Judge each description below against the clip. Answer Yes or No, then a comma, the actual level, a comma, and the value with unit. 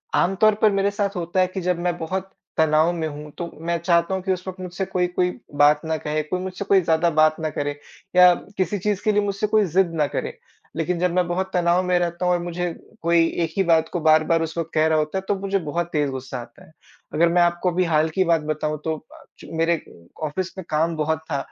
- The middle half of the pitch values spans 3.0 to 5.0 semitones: No, narrow, 2.6 semitones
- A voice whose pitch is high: No, medium, 170 Hz